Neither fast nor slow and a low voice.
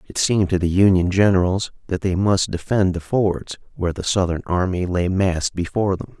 Yes: average, 195 wpm; very low, 90 Hz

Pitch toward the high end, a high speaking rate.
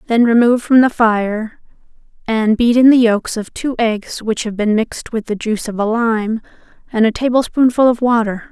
No: high, 230 Hz; average, 195 wpm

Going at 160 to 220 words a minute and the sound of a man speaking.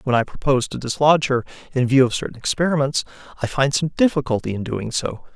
Yes: average, 200 wpm; male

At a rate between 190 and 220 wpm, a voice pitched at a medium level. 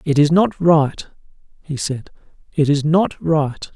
No: average, 160 wpm; medium, 155 Hz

